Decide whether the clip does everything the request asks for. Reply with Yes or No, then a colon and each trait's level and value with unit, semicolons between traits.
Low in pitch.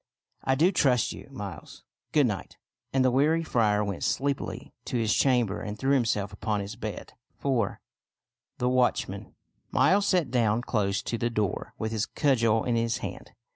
Yes: low, 120 Hz